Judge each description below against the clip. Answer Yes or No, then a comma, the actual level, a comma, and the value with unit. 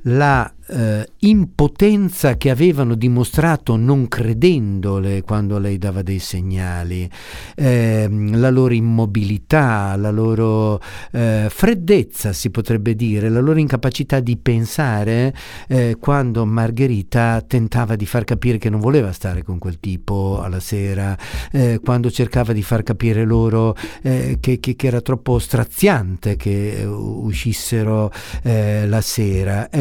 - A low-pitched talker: Yes, low, 115 Hz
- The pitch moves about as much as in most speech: Yes, average, 3.7 semitones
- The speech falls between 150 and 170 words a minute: No, average, 130 wpm